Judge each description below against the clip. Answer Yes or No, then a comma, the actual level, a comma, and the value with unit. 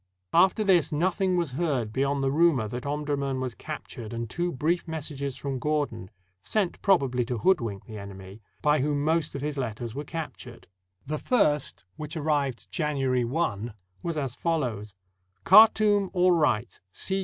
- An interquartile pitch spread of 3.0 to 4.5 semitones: No, average, 5.1 semitones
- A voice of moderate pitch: Yes, medium, 145 Hz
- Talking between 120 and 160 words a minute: Yes, average, 155 wpm